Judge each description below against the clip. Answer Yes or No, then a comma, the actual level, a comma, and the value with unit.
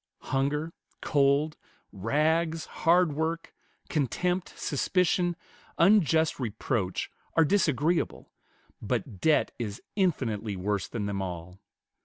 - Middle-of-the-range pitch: Yes, medium, 150 Hz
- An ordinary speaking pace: No, slow, 95 wpm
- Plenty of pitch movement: Yes, wide, 7.4 semitones